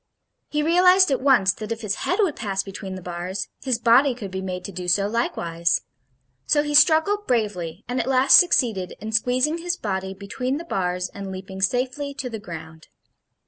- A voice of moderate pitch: No, high, 220 Hz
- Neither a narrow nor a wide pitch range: No, wide, 6.1 semitones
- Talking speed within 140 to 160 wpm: No, average, 190 wpm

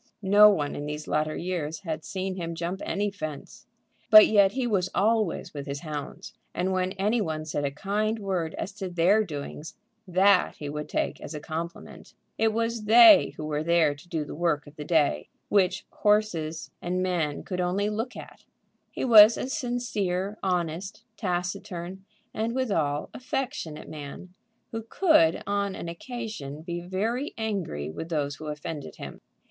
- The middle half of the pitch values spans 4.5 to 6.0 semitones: Yes, average, 5.2 semitones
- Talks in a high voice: No, medium, 180 Hz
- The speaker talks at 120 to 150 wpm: No, average, 170 wpm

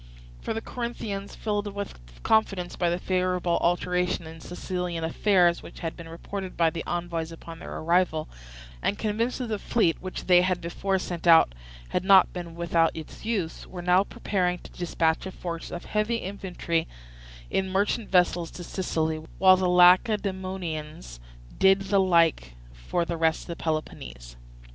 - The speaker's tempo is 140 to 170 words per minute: Yes, average, 160 wpm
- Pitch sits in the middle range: Yes, medium, 180 Hz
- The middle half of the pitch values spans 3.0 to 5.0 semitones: No, narrow, 2.6 semitones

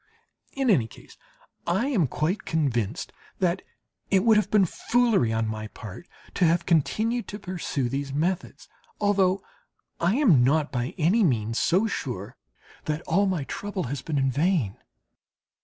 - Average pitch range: No, wide, 6.8 semitones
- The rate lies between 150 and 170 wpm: Yes, average, 155 wpm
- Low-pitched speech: No, medium, 170 Hz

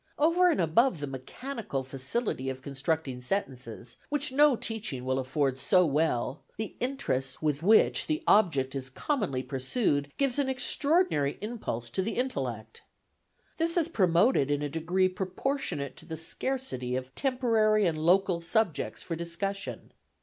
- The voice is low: No, medium, 170 Hz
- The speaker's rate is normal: Yes, average, 145 wpm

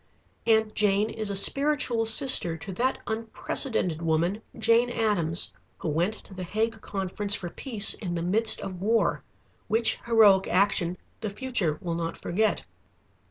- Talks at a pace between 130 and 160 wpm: Yes, average, 150 wpm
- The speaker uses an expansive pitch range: No, average, 3.9 semitones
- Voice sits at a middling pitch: No, high, 205 Hz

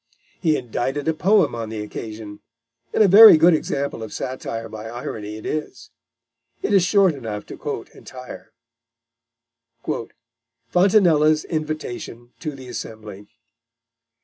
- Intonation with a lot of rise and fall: Yes, wide, 6.3 semitones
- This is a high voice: No, low, 135 Hz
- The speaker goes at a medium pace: No, slow, 125 wpm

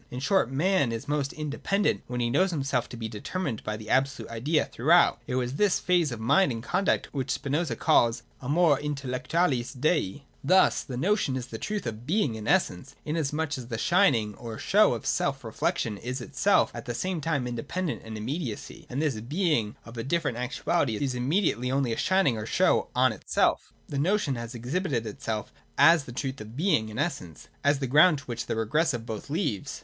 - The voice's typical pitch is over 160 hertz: No, low, 135 Hz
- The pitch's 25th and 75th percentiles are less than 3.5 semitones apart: No, average, 5.3 semitones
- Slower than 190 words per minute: No, average, 200 wpm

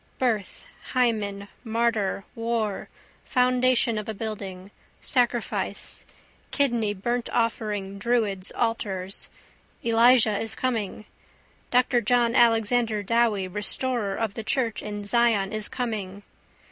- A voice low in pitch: No, high, 225 Hz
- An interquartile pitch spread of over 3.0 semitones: No, average, 2.7 semitones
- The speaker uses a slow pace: Yes, slow, 100 wpm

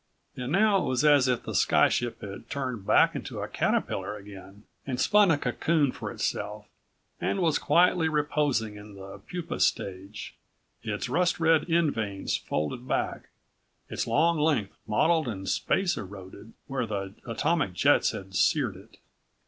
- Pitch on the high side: No, low, 125 Hz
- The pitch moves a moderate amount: No, wide, 8.0 semitones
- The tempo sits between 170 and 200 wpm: No, average, 155 wpm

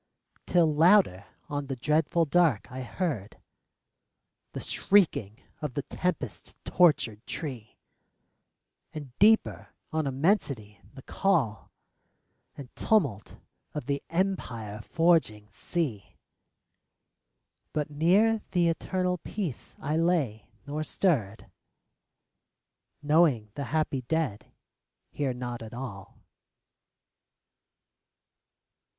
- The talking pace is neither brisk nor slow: No, slow, 95 wpm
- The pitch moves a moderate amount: No, wide, 6.4 semitones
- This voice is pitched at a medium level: Yes, medium, 145 Hz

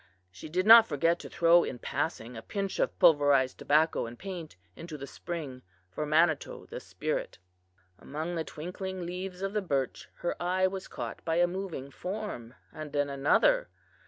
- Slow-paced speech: No, average, 170 wpm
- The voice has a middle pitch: Yes, medium, 165 Hz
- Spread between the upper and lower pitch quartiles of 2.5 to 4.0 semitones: No, average, 4.4 semitones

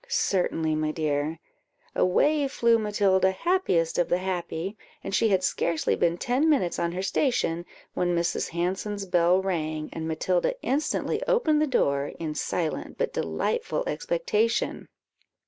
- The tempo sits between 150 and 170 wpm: No, average, 140 wpm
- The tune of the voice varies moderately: No, wide, 7.7 semitones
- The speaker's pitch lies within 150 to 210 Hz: Yes, medium, 185 Hz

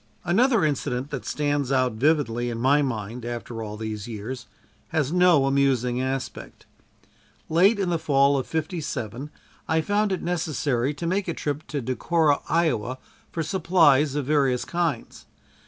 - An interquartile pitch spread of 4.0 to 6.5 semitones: Yes, average, 4.5 semitones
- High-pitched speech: No, medium, 140 Hz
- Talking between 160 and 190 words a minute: No, average, 150 wpm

